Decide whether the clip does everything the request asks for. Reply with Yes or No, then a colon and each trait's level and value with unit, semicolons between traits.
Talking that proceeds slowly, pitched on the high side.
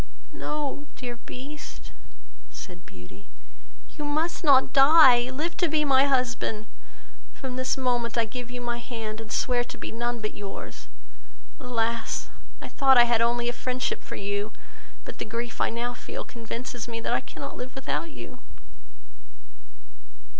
No: average, 155 wpm; high, 245 Hz